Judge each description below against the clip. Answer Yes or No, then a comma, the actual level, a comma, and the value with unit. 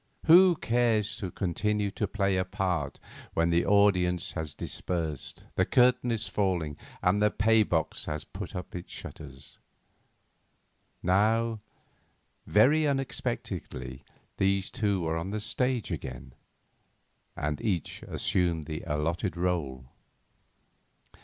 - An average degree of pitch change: Yes, average, 4.7 semitones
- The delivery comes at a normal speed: No, slow, 120 wpm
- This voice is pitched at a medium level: No, very low, 95 Hz